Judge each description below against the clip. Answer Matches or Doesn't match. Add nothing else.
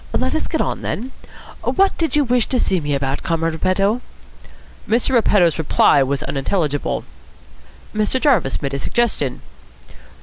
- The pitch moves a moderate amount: Doesn't match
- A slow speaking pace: Doesn't match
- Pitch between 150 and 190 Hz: Matches